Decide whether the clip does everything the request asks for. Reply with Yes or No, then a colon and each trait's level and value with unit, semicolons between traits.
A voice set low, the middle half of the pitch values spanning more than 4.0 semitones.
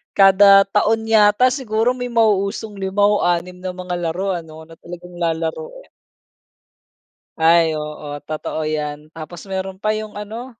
No: high, 190 Hz; average, 4.5 semitones